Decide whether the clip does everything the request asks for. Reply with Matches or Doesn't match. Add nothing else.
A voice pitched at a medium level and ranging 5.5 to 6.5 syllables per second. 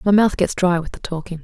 Matches